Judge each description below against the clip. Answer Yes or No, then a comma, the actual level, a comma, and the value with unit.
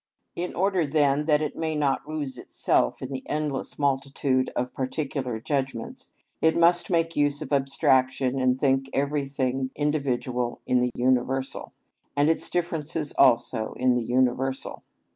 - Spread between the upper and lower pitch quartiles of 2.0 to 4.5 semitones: Yes, narrow, 2.6 semitones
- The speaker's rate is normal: Yes, average, 145 wpm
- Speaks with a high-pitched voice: No, low, 135 Hz